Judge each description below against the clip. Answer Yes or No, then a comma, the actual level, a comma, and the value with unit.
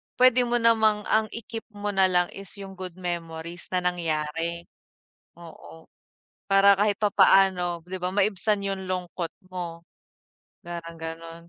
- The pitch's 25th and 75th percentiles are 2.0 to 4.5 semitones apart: Yes, average, 3.1 semitones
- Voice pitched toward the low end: No, medium, 185 Hz